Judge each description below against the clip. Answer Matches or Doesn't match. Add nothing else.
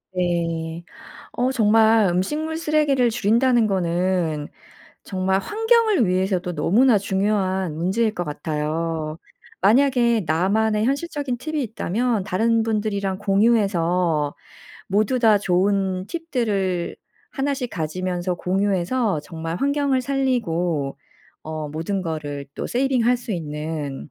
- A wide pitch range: Matches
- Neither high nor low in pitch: Doesn't match